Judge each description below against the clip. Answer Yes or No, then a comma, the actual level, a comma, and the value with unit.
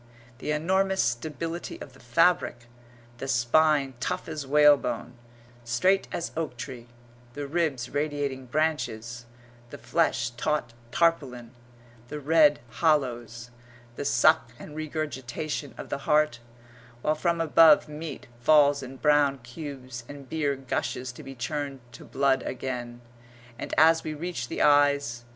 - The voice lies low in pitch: No, medium, 145 Hz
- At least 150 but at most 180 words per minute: No, slow, 135 wpm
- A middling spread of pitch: Yes, average, 4.0 semitones